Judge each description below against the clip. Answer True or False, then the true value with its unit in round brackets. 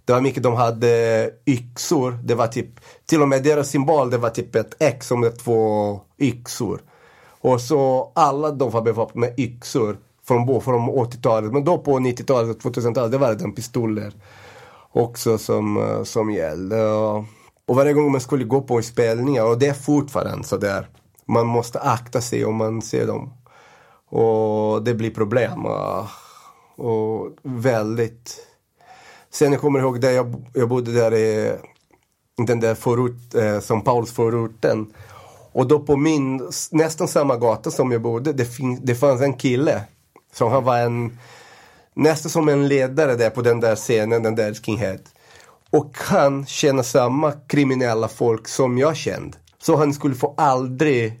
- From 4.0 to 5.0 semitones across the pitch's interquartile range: False (3.4 semitones)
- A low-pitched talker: True (120 Hz)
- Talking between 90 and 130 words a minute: False (160 wpm)